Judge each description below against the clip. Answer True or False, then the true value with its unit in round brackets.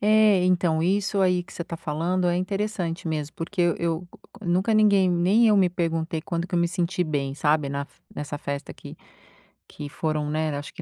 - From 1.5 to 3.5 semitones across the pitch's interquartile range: True (3.1 semitones)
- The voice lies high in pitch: False (175 Hz)